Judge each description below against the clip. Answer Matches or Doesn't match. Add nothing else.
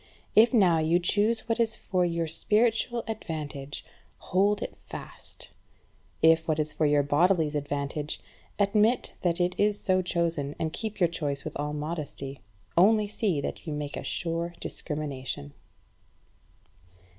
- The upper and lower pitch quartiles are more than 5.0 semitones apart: Matches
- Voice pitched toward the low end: Doesn't match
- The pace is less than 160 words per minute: Matches